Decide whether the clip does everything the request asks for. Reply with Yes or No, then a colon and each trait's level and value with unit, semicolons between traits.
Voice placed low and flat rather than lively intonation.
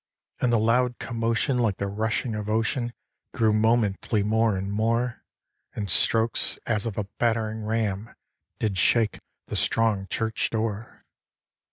Yes: low, 110 Hz; narrow, 1.7 semitones